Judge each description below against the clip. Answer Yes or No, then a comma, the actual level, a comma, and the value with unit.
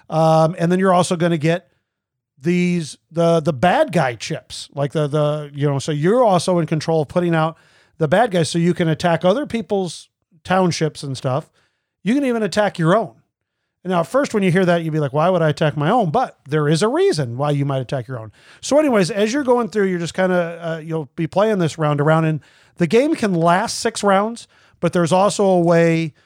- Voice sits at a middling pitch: Yes, medium, 170 Hz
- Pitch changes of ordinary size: Yes, average, 3.4 semitones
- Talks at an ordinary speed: No, fast, 235 wpm